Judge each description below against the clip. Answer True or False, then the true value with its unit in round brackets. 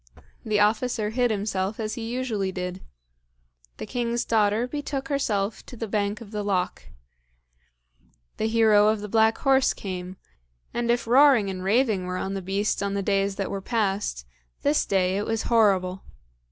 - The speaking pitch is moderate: False (210 Hz)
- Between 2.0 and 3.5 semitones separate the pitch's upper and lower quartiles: True (3.1 semitones)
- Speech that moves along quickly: False (165 wpm)